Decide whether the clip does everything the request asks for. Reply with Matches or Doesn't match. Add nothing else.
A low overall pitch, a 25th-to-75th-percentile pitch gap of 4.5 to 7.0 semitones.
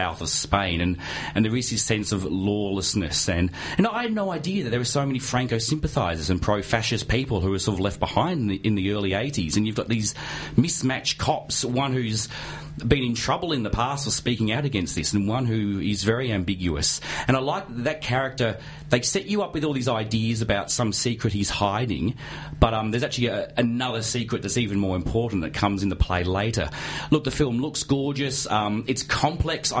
Matches